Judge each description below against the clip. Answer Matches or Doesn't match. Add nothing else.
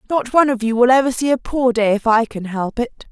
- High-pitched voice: Matches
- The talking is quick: Matches